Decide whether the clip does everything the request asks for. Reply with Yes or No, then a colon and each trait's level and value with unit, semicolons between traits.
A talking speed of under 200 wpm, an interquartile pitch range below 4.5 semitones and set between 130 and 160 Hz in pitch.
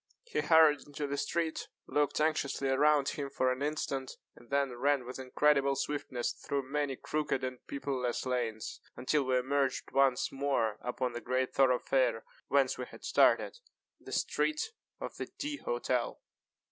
Yes: average, 160 wpm; narrow, 2.4 semitones; low, 135 Hz